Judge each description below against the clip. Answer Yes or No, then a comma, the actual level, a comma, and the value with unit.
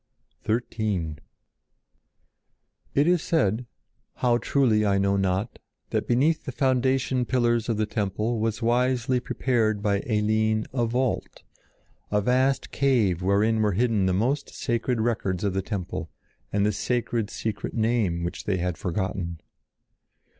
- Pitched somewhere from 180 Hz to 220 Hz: No, low, 110 Hz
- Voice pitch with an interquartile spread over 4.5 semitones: No, average, 3.8 semitones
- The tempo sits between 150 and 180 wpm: No, slow, 135 wpm